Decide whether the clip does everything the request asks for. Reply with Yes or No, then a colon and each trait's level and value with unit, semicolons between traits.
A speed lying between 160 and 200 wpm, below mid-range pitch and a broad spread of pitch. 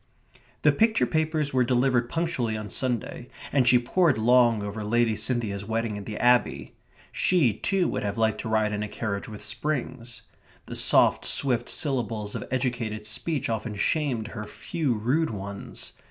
No: average, 165 wpm; low, 120 Hz; average, 3.5 semitones